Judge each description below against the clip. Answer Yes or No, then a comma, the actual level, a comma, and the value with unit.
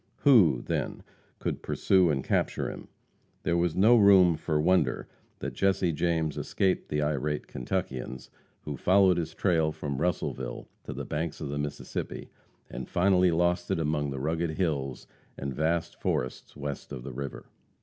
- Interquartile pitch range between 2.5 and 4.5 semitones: Yes, average, 3.7 semitones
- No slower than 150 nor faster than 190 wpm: Yes, average, 160 wpm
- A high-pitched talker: No, very low, 80 Hz